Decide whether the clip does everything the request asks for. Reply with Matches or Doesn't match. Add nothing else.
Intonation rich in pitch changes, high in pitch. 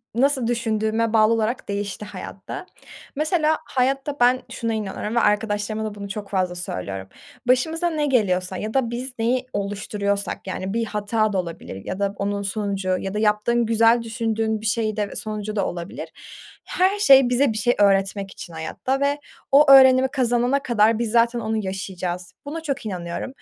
Doesn't match